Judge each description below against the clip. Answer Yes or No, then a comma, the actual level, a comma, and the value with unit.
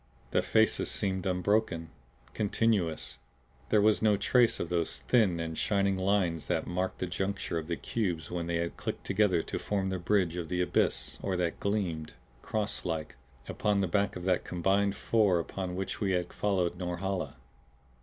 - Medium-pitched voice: No, very low, 95 Hz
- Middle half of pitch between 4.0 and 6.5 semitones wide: No, average, 2.8 semitones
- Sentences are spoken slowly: No, average, 175 wpm